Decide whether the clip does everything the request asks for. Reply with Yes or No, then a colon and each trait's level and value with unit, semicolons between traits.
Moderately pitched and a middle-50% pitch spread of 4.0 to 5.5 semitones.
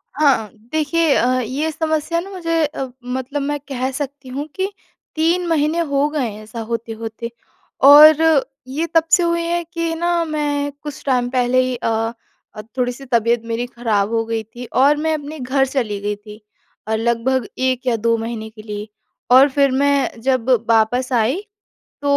No: very high, 260 Hz; average, 4.7 semitones